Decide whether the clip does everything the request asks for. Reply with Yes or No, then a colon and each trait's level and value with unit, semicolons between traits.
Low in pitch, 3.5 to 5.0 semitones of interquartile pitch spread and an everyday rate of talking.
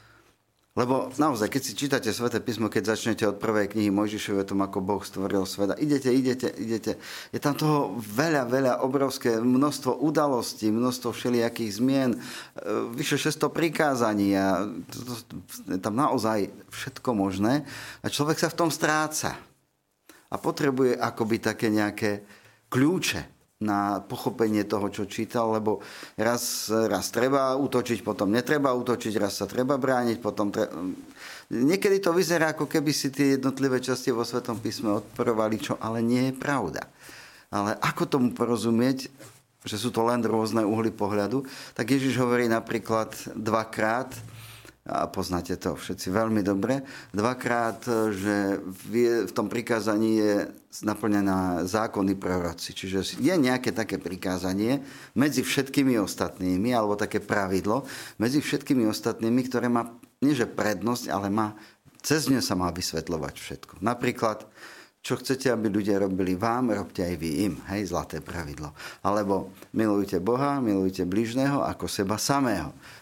Yes: low, 115 Hz; average, 3.9 semitones; average, 140 wpm